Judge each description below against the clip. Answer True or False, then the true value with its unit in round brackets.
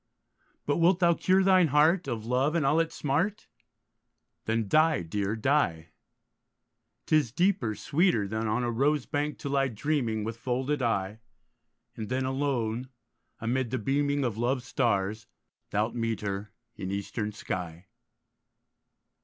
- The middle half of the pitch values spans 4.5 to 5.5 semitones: True (5.2 semitones)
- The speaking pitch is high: False (125 Hz)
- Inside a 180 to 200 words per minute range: False (140 wpm)